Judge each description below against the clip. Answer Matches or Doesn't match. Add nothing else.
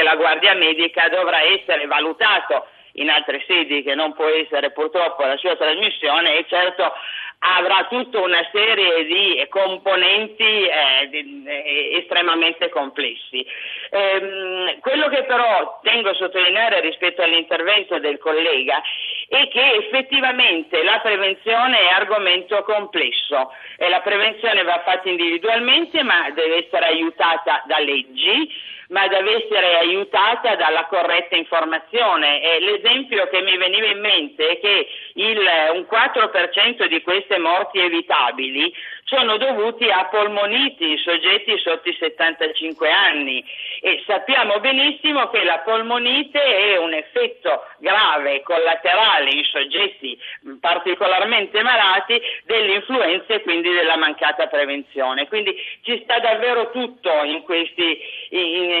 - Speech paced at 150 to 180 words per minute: Doesn't match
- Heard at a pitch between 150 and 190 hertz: Matches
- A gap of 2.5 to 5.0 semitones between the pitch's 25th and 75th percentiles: Doesn't match